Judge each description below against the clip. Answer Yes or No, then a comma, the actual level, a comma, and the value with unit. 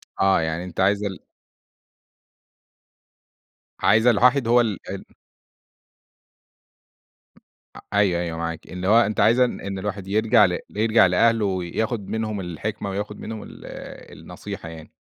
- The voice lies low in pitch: Yes, low, 100 Hz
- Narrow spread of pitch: No, average, 3.4 semitones